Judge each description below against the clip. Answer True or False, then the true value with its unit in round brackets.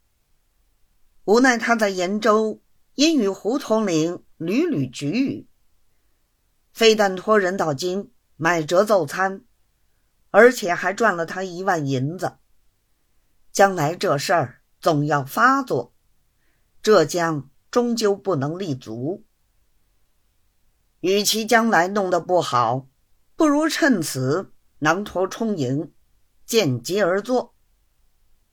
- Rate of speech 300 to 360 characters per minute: False (150 characters per minute)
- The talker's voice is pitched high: False (180 Hz)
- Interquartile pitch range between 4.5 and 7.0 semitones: False (7.4 semitones)